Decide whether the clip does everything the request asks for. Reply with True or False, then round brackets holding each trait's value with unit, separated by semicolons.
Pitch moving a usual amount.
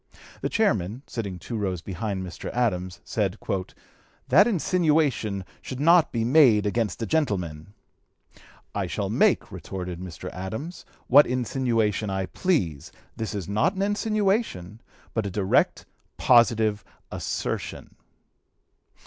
False (6.9 semitones)